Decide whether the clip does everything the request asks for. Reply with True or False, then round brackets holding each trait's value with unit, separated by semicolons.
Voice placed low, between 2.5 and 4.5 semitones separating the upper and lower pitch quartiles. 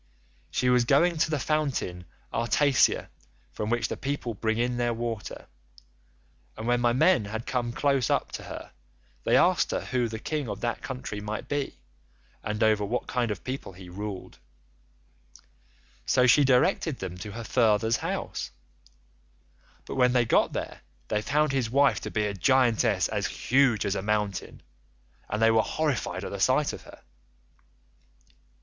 True (120 Hz; 3.9 semitones)